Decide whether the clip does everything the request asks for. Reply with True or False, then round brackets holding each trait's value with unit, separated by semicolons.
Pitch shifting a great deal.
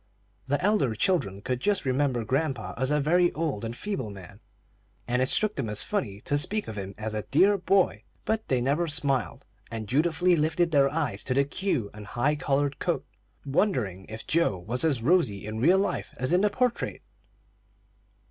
True (7.4 semitones)